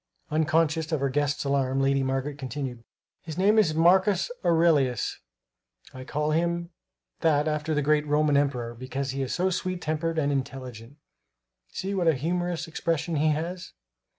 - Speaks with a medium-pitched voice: Yes, medium, 150 Hz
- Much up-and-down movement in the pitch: No, average, 3.4 semitones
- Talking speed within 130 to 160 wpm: Yes, average, 155 wpm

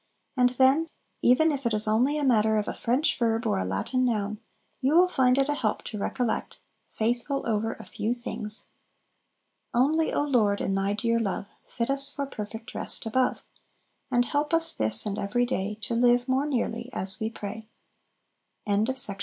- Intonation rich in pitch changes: No, average, 3.8 semitones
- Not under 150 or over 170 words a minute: No, average, 185 wpm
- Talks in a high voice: Yes, high, 235 Hz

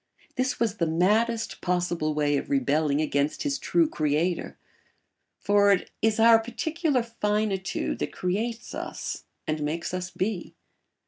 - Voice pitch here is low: No, high, 190 Hz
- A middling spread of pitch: No, wide, 6.5 semitones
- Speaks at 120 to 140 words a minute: Yes, slow, 135 wpm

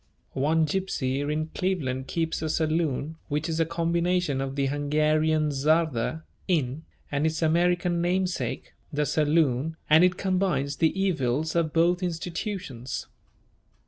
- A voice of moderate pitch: Yes, medium, 160 Hz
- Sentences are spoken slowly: Yes, slow, 130 wpm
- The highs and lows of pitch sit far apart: No, average, 2.9 semitones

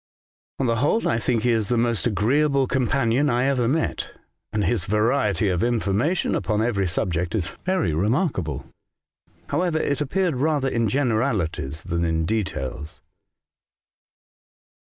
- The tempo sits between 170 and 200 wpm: No, average, 140 wpm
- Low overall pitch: Yes, low, 115 Hz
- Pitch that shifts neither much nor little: No, wide, 5.9 semitones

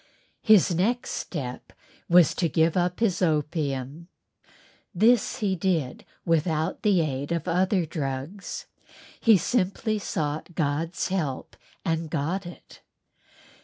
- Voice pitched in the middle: Yes, medium, 170 Hz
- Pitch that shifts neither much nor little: Yes, average, 3.8 semitones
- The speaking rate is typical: No, slow, 115 wpm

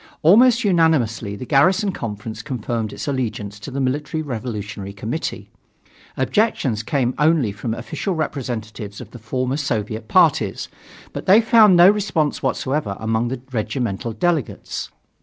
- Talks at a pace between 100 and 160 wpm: Yes, slow, 135 wpm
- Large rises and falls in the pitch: Yes, wide, 6.3 semitones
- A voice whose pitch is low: Yes, low, 130 Hz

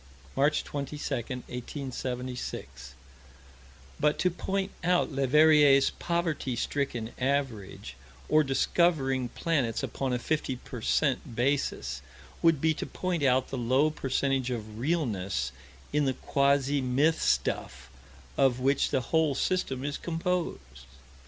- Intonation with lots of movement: No, average, 3.6 semitones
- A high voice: No, low, 135 Hz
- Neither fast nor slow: No, slow, 120 wpm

